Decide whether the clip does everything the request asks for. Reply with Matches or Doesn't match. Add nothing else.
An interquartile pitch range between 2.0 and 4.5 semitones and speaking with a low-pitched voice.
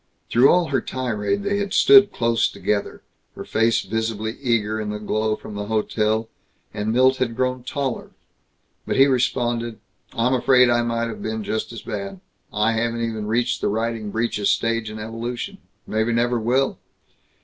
Matches